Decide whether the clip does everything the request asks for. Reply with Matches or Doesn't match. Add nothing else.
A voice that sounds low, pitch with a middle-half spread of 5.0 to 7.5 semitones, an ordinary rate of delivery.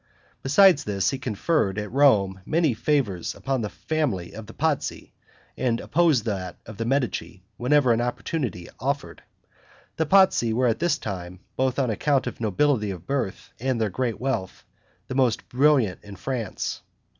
Matches